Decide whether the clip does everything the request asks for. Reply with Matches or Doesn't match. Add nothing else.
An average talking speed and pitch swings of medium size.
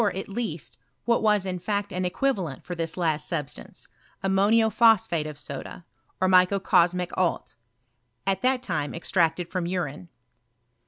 Matches